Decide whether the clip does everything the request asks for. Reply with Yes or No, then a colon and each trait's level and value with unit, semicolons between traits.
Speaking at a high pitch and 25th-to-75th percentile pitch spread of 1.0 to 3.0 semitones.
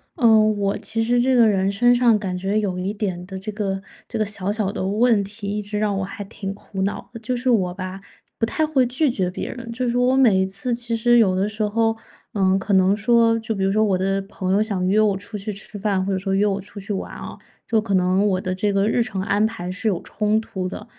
Yes: high, 205 Hz; average, 2.7 semitones